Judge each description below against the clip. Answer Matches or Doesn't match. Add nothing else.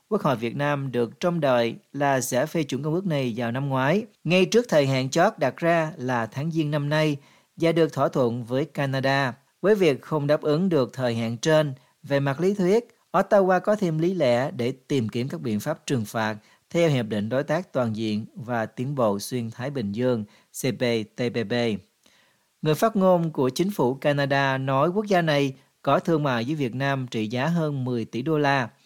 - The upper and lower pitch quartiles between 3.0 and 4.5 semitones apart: Doesn't match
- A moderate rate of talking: Matches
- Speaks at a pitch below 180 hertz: Matches